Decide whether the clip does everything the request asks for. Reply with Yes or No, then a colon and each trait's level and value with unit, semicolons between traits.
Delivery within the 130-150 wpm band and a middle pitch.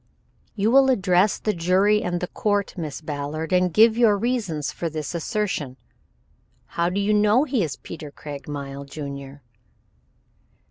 Yes: average, 145 wpm; medium, 180 Hz